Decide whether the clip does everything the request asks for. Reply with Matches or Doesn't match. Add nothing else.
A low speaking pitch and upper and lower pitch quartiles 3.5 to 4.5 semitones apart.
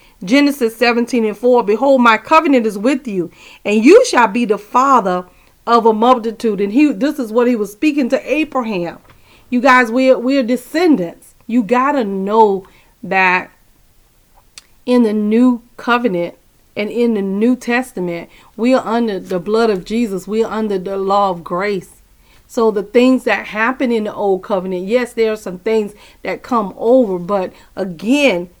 Doesn't match